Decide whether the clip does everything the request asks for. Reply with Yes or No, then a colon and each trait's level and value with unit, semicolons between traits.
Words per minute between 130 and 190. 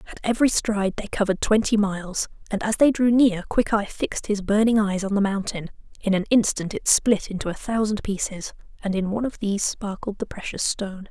No: fast, 205 wpm